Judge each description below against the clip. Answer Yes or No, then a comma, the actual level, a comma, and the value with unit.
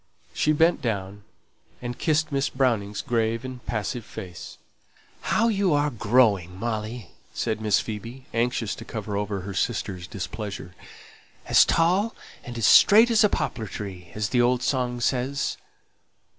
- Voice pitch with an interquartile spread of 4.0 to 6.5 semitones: Yes, average, 4.3 semitones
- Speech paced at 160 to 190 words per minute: No, average, 145 wpm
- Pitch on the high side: No, low, 115 Hz